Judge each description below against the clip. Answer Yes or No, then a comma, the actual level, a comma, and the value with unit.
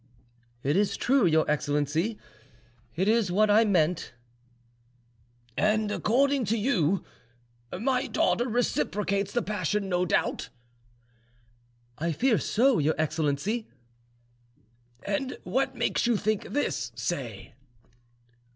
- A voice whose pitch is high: Yes, high, 205 Hz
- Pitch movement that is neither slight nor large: No, wide, 6.1 semitones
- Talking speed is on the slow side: Yes, slow, 105 wpm